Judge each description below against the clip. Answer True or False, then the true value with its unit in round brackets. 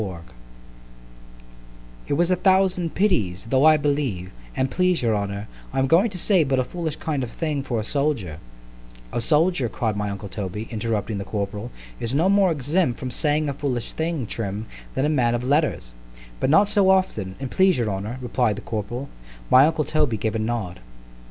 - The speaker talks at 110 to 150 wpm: False (185 wpm)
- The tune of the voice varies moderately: False (7.0 semitones)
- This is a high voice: False (130 Hz)